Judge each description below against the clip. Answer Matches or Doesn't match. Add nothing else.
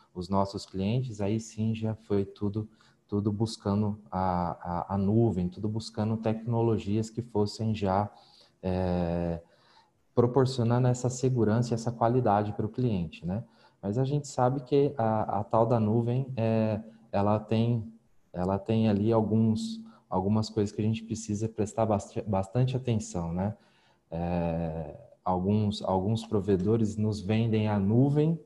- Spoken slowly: Doesn't match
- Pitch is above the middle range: Doesn't match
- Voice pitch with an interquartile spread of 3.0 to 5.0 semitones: Doesn't match